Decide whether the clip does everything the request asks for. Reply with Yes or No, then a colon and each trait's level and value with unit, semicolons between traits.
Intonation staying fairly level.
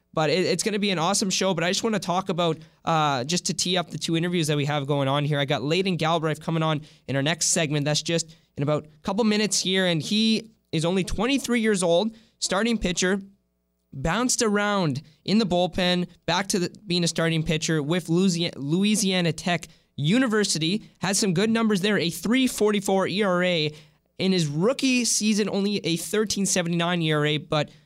No: average, 4.1 semitones